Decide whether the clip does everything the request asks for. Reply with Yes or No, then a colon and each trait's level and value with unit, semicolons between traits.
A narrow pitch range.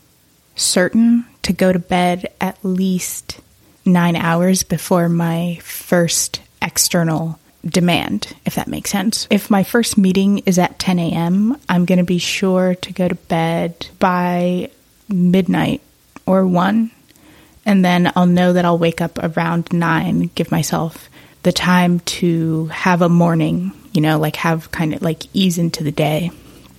Yes: narrow, 2.0 semitones